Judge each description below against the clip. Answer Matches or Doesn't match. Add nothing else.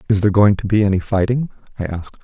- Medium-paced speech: Doesn't match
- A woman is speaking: Doesn't match